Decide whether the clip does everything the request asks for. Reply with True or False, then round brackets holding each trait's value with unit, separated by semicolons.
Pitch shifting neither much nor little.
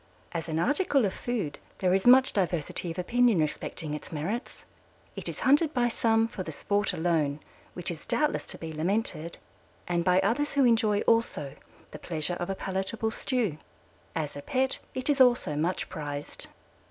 False (7.0 semitones)